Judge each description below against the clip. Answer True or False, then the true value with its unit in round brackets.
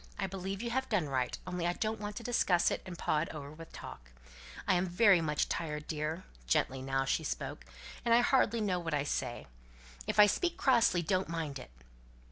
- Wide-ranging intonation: True (5.7 semitones)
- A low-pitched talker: False (175 Hz)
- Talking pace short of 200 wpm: False (205 wpm)